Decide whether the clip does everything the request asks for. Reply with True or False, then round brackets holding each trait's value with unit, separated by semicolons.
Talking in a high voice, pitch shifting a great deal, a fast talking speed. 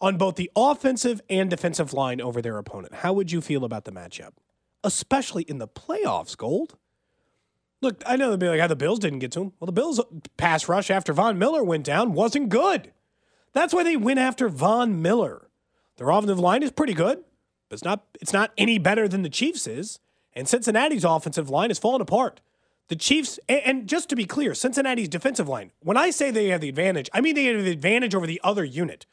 True (195 Hz; 6.7 semitones; 215 wpm)